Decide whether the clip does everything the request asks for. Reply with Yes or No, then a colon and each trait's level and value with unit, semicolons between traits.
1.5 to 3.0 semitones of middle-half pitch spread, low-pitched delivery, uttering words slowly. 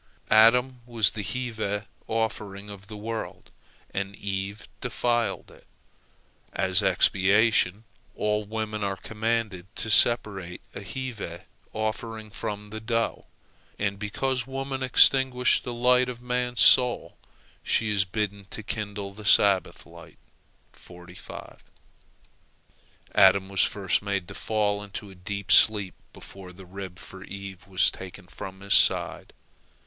Yes: average, 2.7 semitones; low, 105 Hz; slow, 125 wpm